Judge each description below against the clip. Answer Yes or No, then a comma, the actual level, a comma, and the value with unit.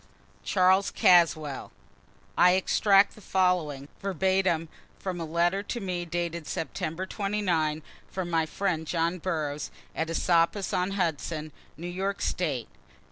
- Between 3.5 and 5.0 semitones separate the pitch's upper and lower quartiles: No, average, 2.7 semitones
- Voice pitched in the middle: Yes, medium, 175 Hz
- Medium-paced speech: No, slow, 125 wpm